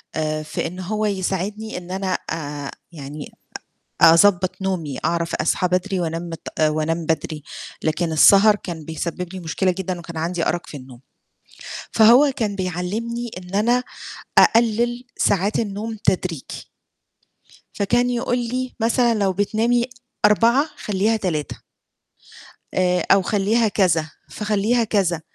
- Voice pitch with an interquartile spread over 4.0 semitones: Yes, average, 4.6 semitones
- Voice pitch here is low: No, high, 190 Hz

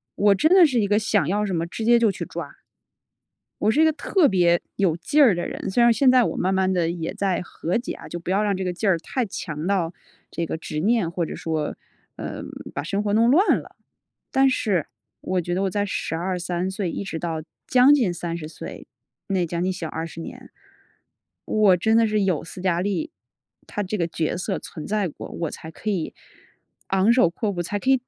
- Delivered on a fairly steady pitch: No, average, 4.3 semitones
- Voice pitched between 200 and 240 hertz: No, high, 190 Hz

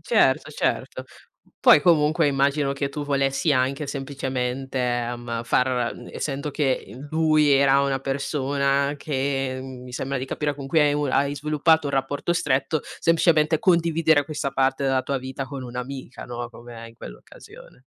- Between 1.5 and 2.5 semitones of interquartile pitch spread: Yes, narrow, 2.1 semitones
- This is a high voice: No, medium, 140 Hz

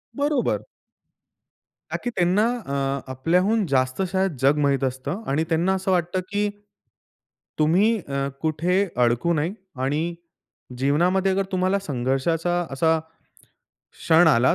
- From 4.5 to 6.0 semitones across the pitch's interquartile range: Yes, wide, 5.5 semitones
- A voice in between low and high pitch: Yes, medium, 170 Hz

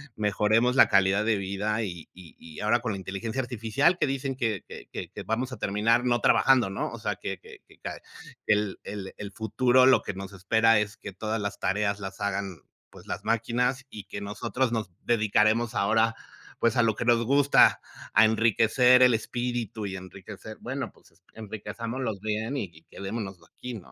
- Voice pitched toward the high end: No, low, 110 Hz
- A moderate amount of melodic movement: Yes, average, 3.1 semitones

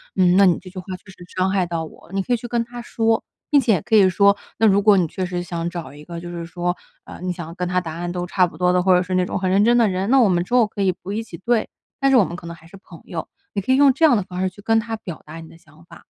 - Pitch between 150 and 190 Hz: Yes, medium, 185 Hz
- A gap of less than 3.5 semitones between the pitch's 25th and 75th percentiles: No, average, 4.0 semitones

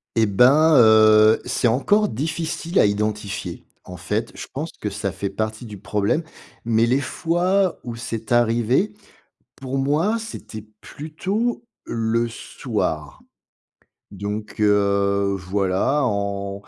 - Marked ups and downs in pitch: Yes, wide, 6.5 semitones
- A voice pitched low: Yes, low, 115 Hz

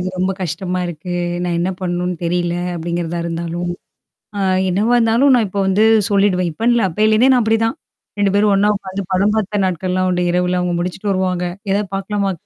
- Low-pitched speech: No, medium, 185 Hz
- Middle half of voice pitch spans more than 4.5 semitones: No, average, 2.7 semitones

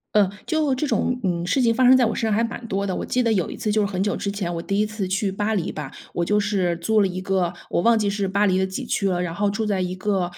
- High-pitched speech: Yes, high, 200 Hz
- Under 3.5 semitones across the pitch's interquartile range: Yes, average, 2.9 semitones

